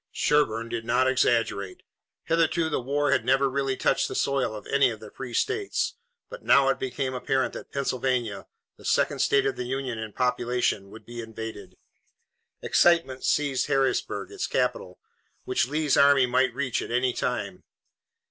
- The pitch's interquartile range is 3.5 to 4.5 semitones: No, average, 2.9 semitones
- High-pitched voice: No, low, 130 Hz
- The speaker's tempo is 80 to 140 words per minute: No, average, 165 wpm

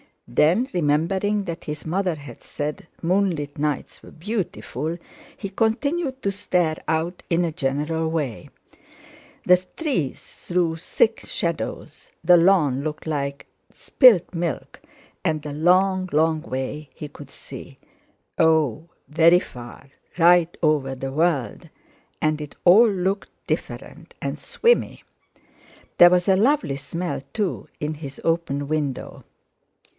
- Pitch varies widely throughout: No, average, 3.7 semitones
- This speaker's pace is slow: Yes, slow, 125 wpm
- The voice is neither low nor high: Yes, medium, 165 Hz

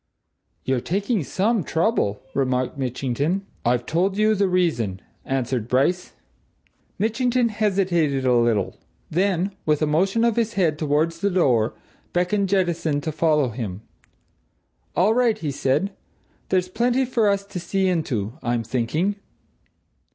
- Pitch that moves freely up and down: Yes, wide, 7.2 semitones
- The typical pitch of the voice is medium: Yes, medium, 170 Hz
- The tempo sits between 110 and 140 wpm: Yes, slow, 135 wpm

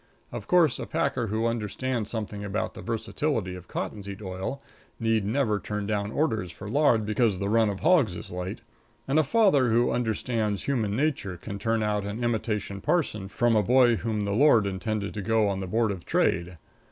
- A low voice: Yes, low, 110 Hz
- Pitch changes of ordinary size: Yes, average, 3.1 semitones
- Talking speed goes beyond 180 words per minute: Yes, average, 190 wpm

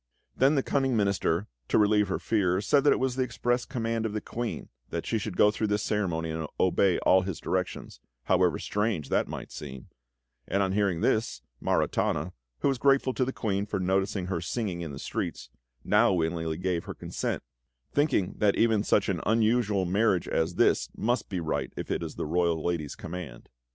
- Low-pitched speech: Yes, low, 100 Hz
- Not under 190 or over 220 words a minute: Yes, average, 195 wpm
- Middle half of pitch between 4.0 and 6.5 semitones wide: Yes, average, 4.4 semitones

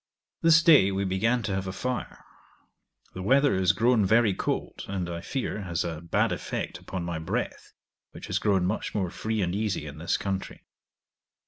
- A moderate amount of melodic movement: Yes, average, 3.6 semitones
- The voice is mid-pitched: No, very low, 95 Hz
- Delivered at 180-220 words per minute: Yes, average, 185 wpm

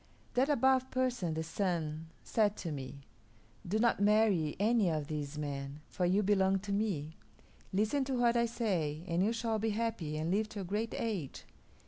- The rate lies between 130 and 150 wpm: No, average, 180 wpm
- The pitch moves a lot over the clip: Yes, wide, 6.1 semitones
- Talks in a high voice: Yes, high, 200 Hz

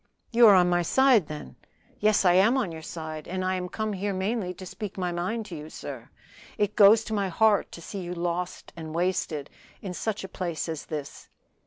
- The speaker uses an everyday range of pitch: Yes, average, 3.5 semitones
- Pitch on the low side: No, medium, 185 Hz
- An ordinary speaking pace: No, fast, 215 wpm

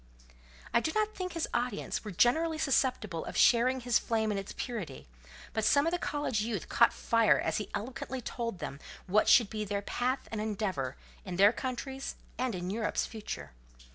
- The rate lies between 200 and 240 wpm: No, average, 185 wpm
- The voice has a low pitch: No, high, 230 Hz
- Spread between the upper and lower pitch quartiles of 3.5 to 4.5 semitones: Yes, average, 4.1 semitones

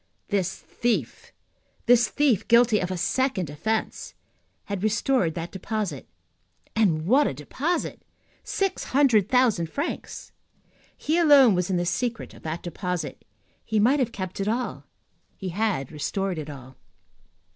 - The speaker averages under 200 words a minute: Yes, average, 140 wpm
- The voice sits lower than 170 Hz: No, high, 205 Hz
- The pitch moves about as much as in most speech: No, wide, 5.9 semitones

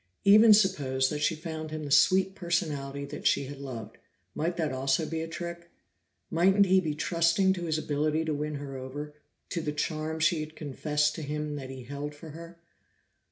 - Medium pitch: Yes, medium, 155 Hz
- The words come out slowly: No, average, 195 wpm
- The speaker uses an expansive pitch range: No, average, 2.8 semitones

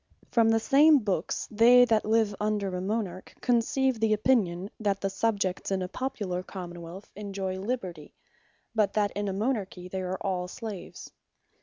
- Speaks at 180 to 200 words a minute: No, average, 165 wpm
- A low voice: No, high, 205 Hz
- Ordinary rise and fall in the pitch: Yes, average, 3.3 semitones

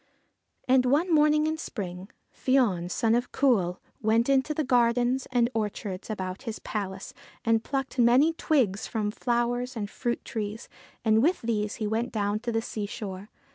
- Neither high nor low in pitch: No, high, 230 Hz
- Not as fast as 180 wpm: Yes, average, 160 wpm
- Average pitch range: Yes, average, 3.7 semitones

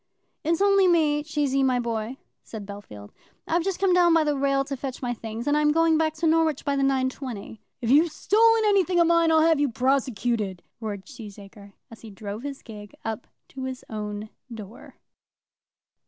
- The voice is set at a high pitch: Yes, very high, 270 Hz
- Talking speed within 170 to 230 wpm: Yes, average, 185 wpm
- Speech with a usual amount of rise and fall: No, wide, 6.3 semitones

